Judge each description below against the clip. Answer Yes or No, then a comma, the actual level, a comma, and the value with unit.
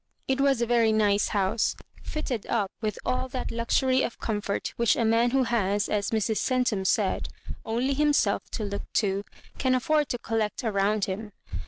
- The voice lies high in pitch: Yes, high, 225 Hz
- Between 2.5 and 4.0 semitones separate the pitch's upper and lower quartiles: Yes, average, 3.6 semitones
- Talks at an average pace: Yes, average, 175 wpm